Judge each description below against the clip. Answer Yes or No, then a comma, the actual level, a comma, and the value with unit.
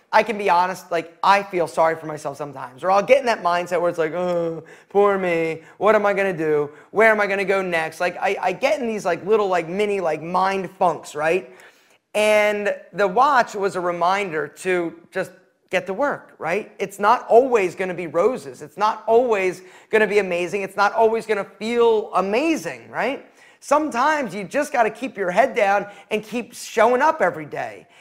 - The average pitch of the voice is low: No, high, 195 Hz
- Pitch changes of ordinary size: Yes, average, 3.9 semitones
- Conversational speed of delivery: No, fast, 210 wpm